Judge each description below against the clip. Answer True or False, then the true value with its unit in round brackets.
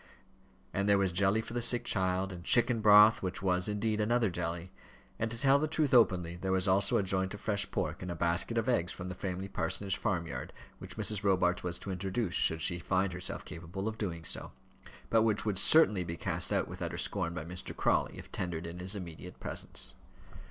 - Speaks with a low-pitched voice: True (95 Hz)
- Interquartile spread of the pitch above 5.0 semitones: False (3.2 semitones)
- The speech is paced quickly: True (215 wpm)